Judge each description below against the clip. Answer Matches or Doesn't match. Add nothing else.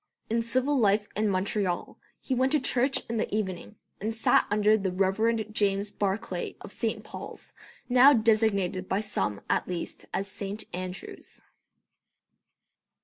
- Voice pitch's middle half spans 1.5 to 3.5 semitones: Matches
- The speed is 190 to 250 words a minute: Doesn't match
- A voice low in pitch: Doesn't match